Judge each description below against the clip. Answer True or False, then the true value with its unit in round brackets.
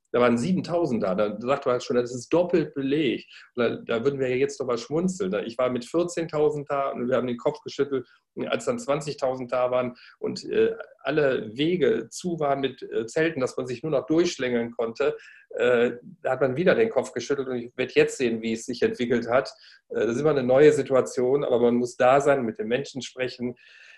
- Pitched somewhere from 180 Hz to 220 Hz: False (140 Hz)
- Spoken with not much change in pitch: False (4.8 semitones)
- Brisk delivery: True (205 wpm)